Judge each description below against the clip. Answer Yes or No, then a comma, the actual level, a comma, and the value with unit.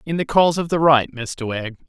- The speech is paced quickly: Yes, fast, 255 wpm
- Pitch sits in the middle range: Yes, medium, 145 Hz